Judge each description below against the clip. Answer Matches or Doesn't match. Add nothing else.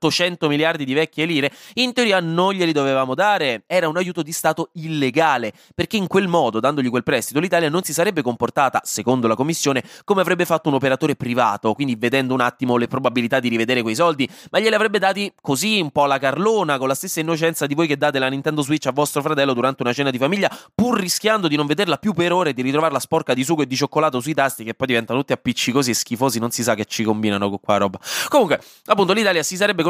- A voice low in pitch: Doesn't match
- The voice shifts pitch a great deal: Doesn't match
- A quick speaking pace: Matches